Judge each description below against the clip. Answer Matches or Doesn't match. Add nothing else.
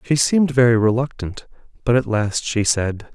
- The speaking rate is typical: Matches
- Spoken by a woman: Doesn't match